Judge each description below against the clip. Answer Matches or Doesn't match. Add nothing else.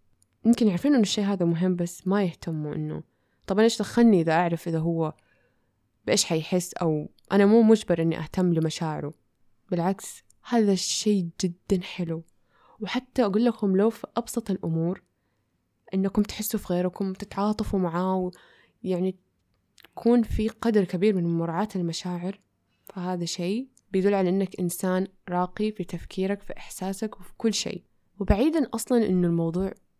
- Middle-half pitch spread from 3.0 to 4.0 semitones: Matches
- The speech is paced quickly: Matches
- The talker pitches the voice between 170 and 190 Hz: Matches